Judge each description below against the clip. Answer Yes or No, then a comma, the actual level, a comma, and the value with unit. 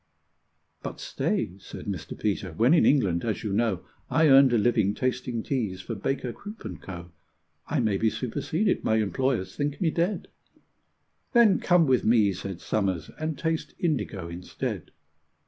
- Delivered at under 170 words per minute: Yes, average, 160 wpm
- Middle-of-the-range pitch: No, low, 115 Hz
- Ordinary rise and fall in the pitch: No, wide, 6.7 semitones